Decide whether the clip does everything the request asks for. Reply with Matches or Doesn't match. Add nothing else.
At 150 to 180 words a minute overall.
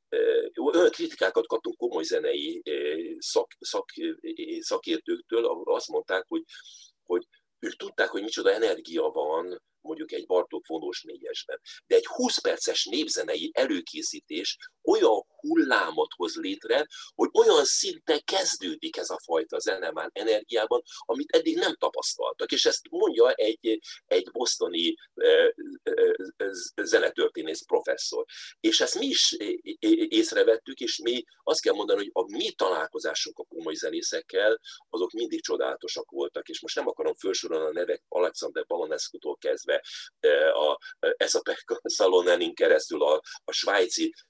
Doesn't match